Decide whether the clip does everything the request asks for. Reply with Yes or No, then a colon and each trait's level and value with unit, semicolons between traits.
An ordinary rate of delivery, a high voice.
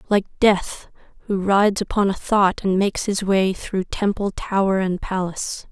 Yes: average, 170 wpm; high, 195 Hz